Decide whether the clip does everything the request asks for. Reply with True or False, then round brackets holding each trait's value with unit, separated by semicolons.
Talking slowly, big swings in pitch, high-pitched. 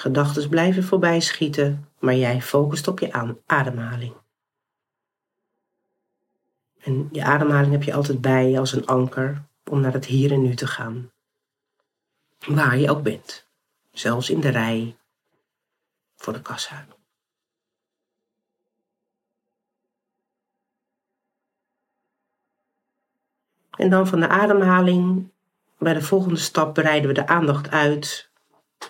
False (110 wpm; 6.0 semitones; 150 Hz)